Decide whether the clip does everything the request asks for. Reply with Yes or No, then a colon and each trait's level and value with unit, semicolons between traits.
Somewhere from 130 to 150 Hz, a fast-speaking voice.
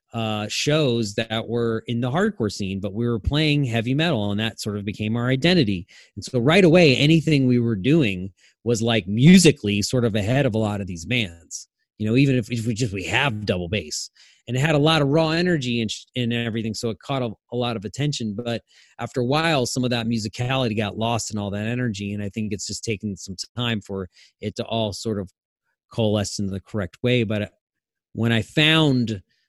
No: low, 115 Hz; fast, 220 wpm